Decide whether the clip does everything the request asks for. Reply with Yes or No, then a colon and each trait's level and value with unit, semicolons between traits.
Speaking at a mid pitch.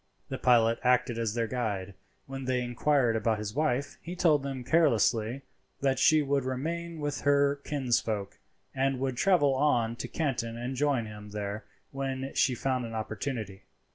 No: low, 130 Hz